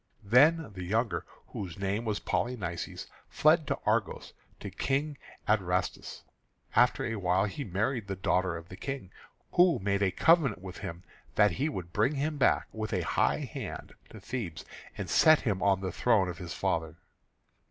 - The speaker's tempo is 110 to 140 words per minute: No, average, 175 wpm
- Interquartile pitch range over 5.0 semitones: Yes, wide, 5.6 semitones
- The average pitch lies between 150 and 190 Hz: No, low, 100 Hz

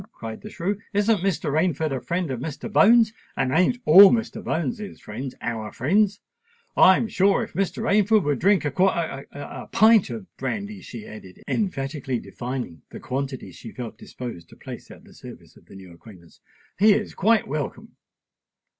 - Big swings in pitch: Yes, wide, 8.0 semitones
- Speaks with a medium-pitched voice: Yes, medium, 160 Hz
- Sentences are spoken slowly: No, average, 165 wpm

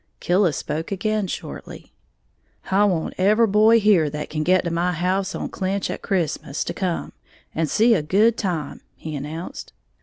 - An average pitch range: Yes, average, 4.3 semitones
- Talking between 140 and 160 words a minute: No, average, 170 wpm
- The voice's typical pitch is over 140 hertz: Yes, medium, 185 Hz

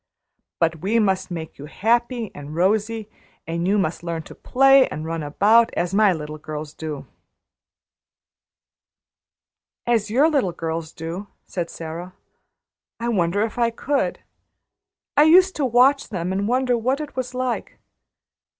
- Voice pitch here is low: No, high, 205 Hz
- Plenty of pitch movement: Yes, wide, 6.6 semitones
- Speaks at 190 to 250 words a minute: No, average, 150 wpm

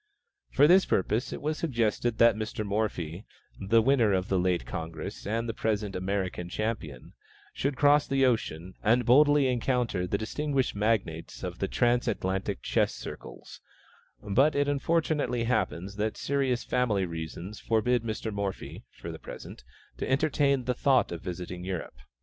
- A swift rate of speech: No, average, 150 wpm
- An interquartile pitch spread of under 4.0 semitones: No, wide, 5.4 semitones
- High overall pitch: No, low, 110 Hz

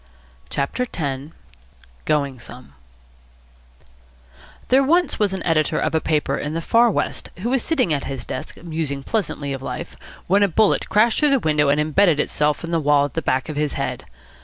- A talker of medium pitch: Yes, medium, 155 Hz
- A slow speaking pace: No, average, 185 wpm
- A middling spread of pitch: No, wide, 6.4 semitones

